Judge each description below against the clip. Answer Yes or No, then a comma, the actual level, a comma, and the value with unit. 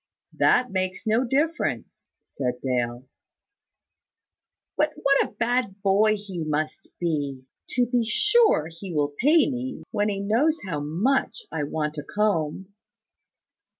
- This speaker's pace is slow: Yes, slow, 130 wpm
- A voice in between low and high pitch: No, high, 195 Hz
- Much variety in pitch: Yes, wide, 8.3 semitones